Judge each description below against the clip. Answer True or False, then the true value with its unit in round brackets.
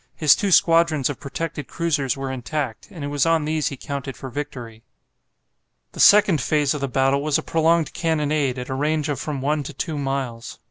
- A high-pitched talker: False (145 Hz)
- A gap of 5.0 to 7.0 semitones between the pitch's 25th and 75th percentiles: False (2.7 semitones)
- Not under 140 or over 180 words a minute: False (200 wpm)